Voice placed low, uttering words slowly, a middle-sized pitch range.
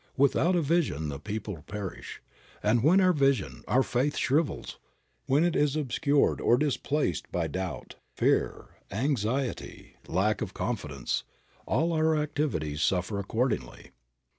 No: low, 130 Hz; slow, 130 wpm; wide, 7.7 semitones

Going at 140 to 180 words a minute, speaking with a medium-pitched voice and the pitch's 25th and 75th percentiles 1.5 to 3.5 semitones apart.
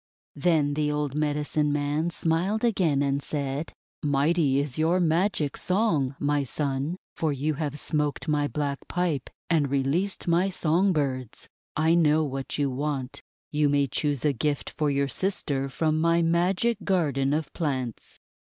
Yes: average, 155 wpm; medium, 150 Hz; average, 3.0 semitones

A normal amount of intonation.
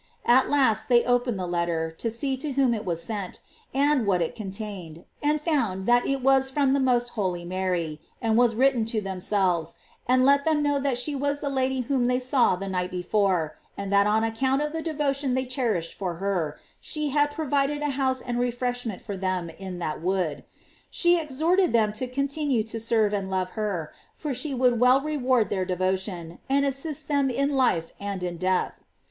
No: wide, 6.3 semitones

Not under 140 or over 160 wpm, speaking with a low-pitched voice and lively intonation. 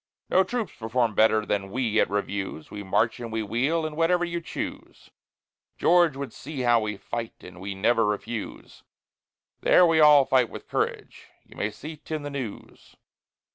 No: average, 175 wpm; low, 120 Hz; wide, 6.6 semitones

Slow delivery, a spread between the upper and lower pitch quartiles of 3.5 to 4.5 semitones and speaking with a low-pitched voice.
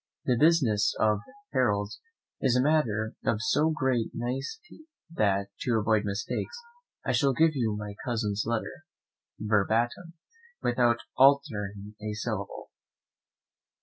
Yes: slow, 115 wpm; average, 4.2 semitones; low, 115 Hz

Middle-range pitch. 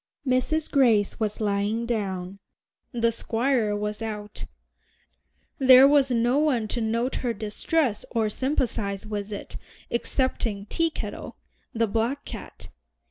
No: high, 230 Hz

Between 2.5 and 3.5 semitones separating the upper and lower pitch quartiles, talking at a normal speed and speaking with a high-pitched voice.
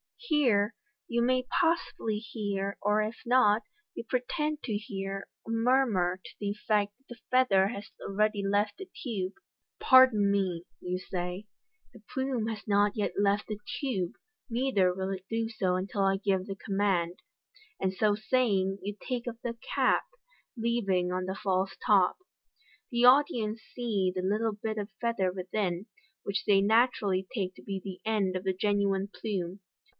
Yes: average, 3.2 semitones; average, 170 wpm; high, 205 Hz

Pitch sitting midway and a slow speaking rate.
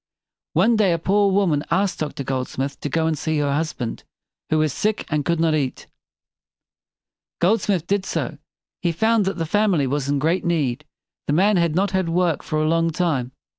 No: medium, 165 Hz; average, 190 wpm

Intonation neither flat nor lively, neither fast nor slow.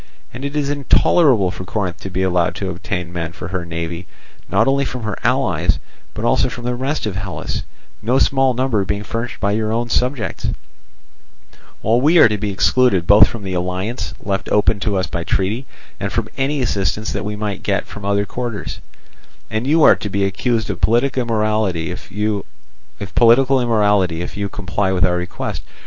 Yes: average, 4.3 semitones; average, 180 wpm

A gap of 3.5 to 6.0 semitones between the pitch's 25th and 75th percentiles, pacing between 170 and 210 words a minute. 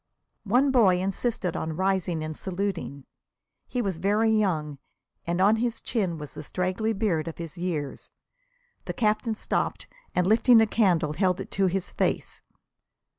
No: average, 4.4 semitones; average, 155 wpm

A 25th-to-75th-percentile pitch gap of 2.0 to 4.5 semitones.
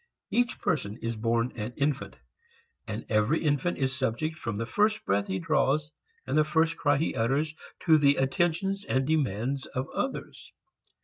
No: average, 5.3 semitones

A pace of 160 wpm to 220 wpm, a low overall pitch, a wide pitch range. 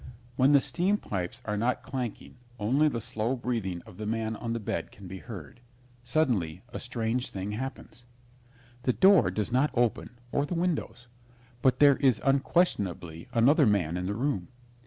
No: average, 170 wpm; low, 120 Hz; average, 4.7 semitones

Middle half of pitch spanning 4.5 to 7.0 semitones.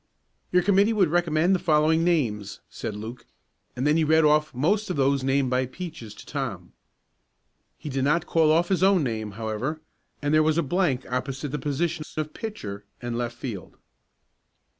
Yes: average, 5.0 semitones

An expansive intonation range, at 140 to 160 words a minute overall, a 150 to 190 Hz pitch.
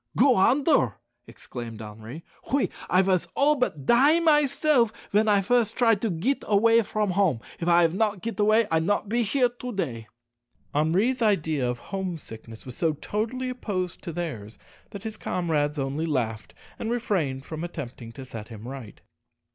No: wide, 8.2 semitones; average, 170 wpm; medium, 185 Hz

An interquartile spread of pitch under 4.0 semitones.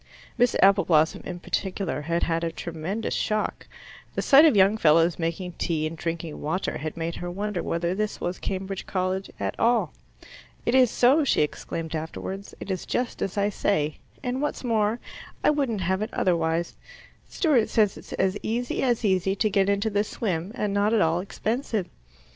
No: average, 4.3 semitones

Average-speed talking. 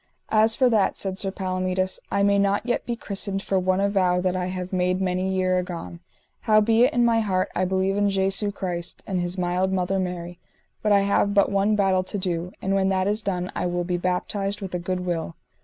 No: fast, 220 wpm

